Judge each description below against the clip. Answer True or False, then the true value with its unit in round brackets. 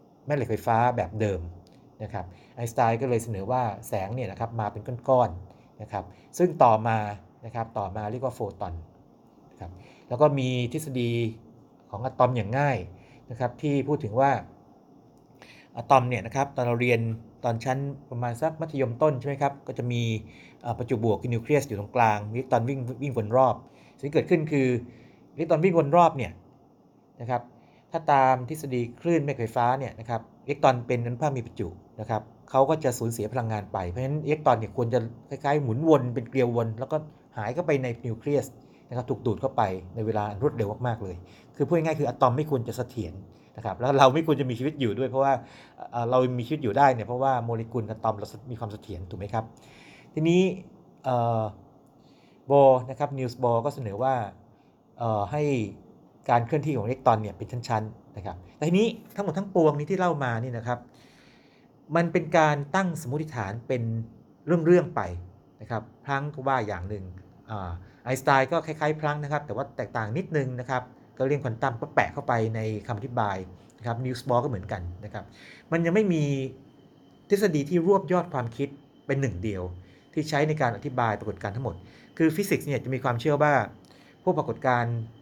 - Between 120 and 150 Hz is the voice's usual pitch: True (125 Hz)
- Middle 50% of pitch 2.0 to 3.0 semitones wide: False (4.0 semitones)